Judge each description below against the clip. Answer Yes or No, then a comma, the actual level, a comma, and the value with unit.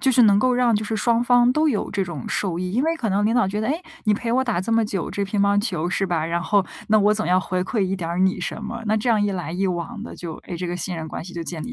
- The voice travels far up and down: No, average, 4.1 semitones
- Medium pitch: No, high, 205 Hz